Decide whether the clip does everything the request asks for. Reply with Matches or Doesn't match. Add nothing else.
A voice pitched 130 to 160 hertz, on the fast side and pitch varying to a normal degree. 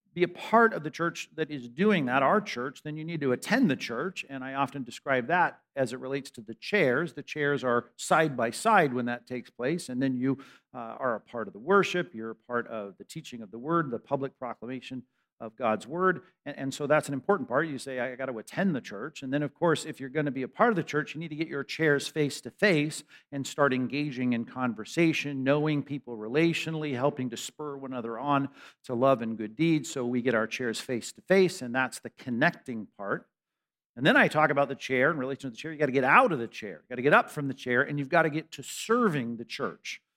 Matches